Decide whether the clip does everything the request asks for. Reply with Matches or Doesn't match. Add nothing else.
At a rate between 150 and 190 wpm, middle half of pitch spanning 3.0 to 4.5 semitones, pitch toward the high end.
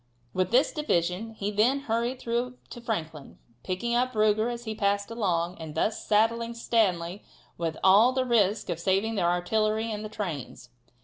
Matches